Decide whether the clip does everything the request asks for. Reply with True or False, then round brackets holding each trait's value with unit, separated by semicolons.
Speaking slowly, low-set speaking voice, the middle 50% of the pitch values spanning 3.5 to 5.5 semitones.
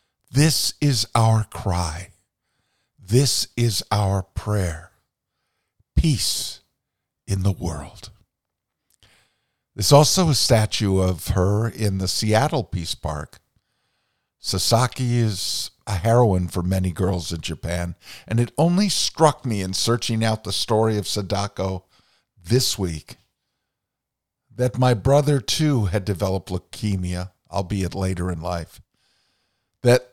True (115 wpm; 105 Hz; 4.5 semitones)